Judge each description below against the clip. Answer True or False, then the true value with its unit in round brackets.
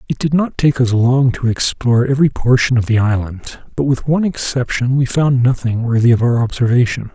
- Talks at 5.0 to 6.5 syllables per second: True (5.5 syllables/s)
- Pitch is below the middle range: True (125 Hz)